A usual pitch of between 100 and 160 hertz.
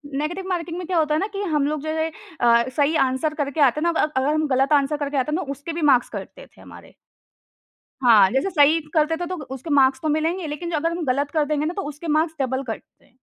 No: very high, 300 Hz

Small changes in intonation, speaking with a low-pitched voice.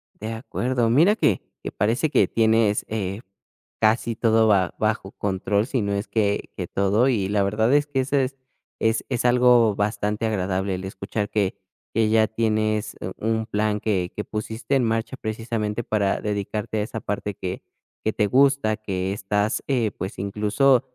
Yes: narrow, 2.1 semitones; low, 110 Hz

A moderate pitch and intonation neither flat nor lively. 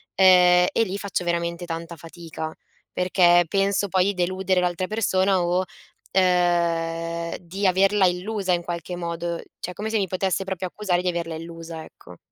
No: medium, 180 Hz; narrow, 1.9 semitones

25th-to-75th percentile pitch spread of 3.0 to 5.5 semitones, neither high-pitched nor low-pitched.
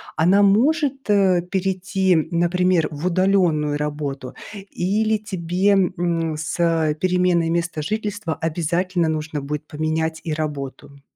Yes: average, 3.4 semitones; medium, 170 Hz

